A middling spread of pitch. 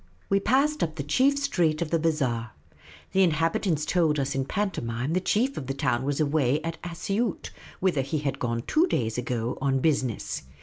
No: wide, 5.7 semitones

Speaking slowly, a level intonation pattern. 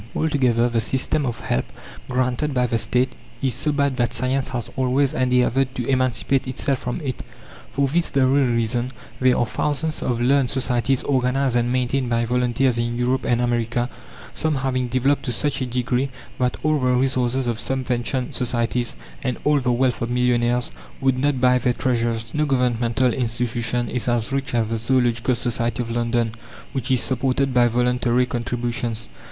No: average, 170 wpm; narrow, 1.8 semitones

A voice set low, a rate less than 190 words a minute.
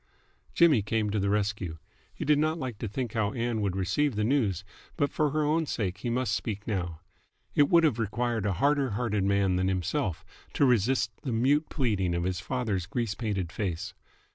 No: low, 110 Hz; average, 195 wpm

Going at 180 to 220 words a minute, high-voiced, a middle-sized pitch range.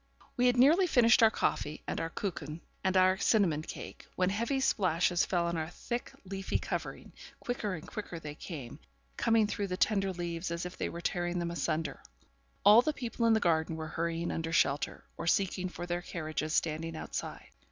No: average, 190 wpm; medium, 175 Hz; average, 4.2 semitones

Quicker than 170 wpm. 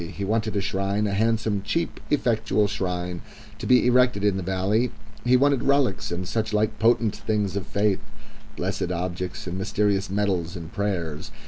No: average, 165 wpm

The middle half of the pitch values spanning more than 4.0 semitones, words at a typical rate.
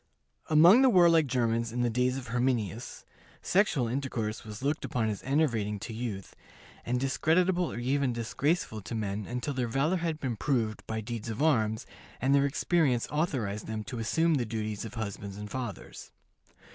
Yes: average, 4.5 semitones; average, 170 wpm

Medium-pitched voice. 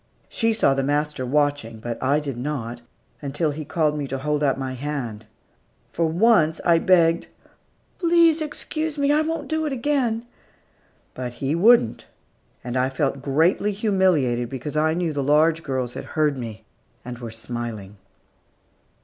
Yes: medium, 150 Hz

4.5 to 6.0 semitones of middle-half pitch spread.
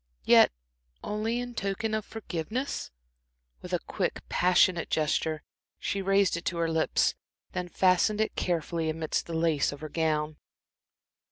No: average, 4.0 semitones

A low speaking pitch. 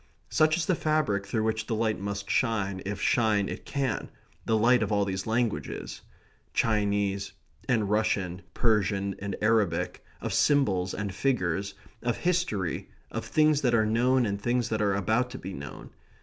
Yes: low, 110 Hz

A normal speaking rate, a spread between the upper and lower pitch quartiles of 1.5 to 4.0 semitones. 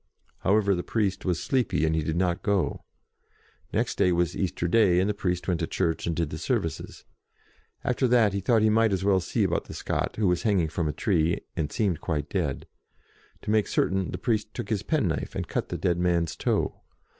No: fast, 220 wpm; average, 3.7 semitones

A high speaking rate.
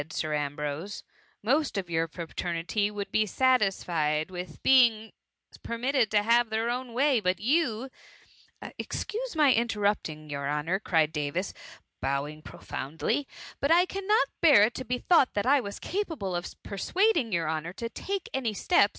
No: average, 165 wpm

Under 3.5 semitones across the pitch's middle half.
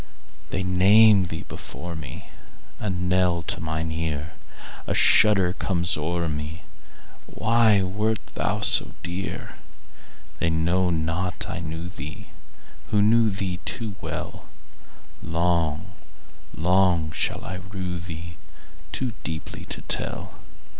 Yes: average, 2.9 semitones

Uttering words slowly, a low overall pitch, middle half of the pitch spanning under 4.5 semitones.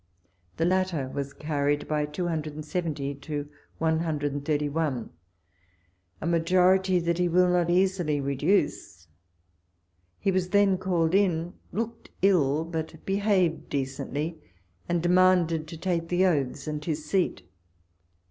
No: slow, 120 wpm; medium, 165 Hz; average, 3.5 semitones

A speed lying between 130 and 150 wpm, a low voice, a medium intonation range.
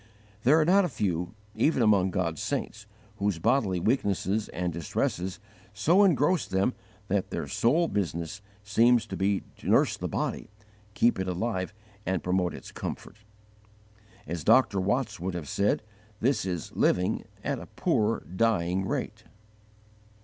Yes: average, 145 wpm; low, 100 Hz; average, 4.5 semitones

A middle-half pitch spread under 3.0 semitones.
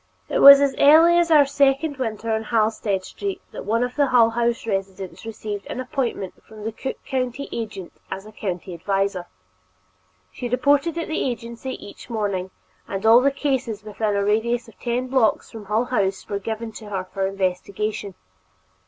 No: average, 4.3 semitones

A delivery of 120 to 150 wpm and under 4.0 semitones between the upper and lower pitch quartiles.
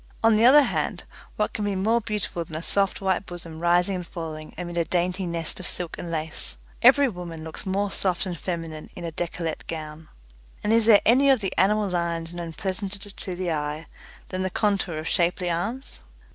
No: average, 200 wpm; average, 3.3 semitones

